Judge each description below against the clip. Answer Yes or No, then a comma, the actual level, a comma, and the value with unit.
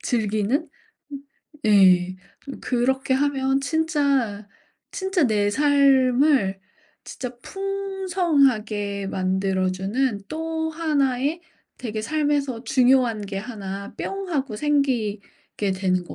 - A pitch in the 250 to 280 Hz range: Yes, very high, 255 Hz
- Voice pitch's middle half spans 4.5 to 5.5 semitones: No, wide, 6.1 semitones